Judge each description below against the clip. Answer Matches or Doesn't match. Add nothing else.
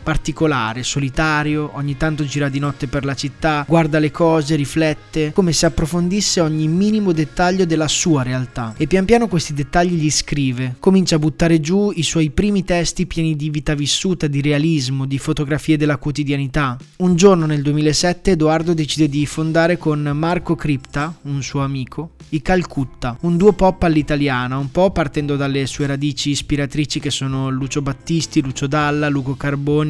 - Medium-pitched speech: Matches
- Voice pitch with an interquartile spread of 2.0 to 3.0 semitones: Matches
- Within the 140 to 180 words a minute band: Matches